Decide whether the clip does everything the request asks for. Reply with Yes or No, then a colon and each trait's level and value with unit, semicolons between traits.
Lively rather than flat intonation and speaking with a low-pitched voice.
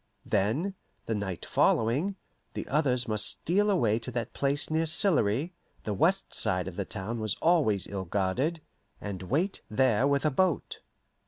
Yes: wide, 7.7 semitones; low, 125 Hz